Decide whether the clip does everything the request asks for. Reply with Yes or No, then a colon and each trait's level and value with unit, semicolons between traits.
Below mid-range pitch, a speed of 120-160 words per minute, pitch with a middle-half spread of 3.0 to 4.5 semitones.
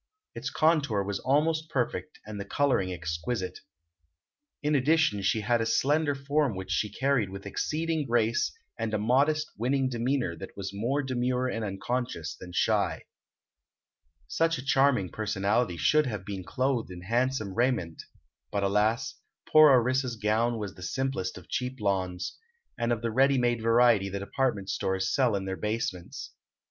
No: low, 115 Hz; average, 155 wpm; average, 5.2 semitones